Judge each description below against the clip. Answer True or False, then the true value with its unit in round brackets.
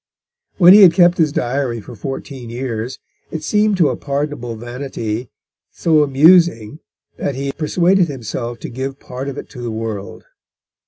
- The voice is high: False (135 Hz)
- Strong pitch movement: False (5.0 semitones)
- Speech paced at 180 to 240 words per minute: False (160 wpm)